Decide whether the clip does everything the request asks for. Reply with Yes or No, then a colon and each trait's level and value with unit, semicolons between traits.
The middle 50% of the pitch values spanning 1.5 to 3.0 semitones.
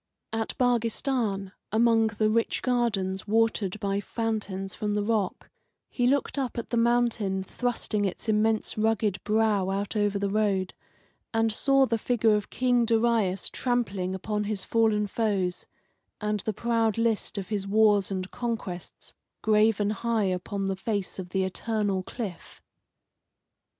Yes: narrow, 2.6 semitones